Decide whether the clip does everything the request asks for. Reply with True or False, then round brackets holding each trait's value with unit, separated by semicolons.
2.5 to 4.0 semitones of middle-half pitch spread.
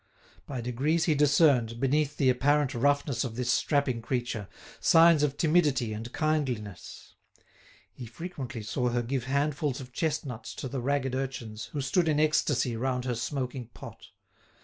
True (3.4 semitones)